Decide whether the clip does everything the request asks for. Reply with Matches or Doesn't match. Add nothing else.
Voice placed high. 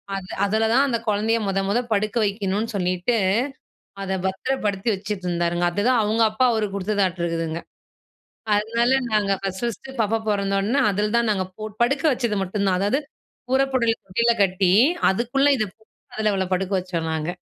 Matches